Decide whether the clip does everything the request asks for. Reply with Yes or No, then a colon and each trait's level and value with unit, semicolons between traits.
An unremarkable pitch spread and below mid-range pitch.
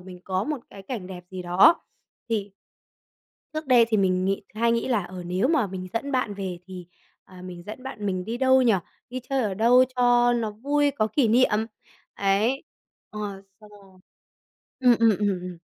No: average, 4.7 semitones; high, 215 Hz